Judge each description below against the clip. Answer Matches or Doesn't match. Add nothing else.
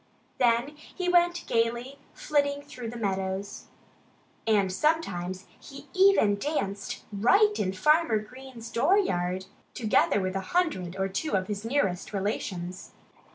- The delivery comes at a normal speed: Doesn't match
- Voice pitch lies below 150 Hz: Doesn't match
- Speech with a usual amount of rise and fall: Doesn't match